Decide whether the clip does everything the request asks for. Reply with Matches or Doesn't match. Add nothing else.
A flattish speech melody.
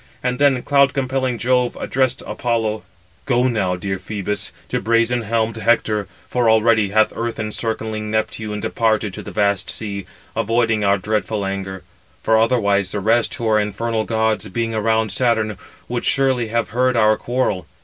Matches